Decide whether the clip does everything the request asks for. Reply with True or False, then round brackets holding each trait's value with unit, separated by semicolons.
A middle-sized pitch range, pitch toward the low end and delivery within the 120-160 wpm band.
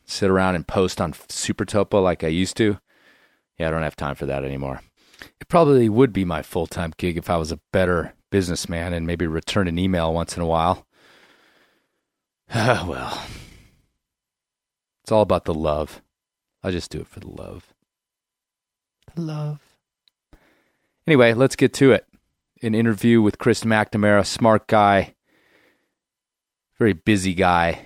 True (4.8 semitones; 95 Hz; 155 wpm)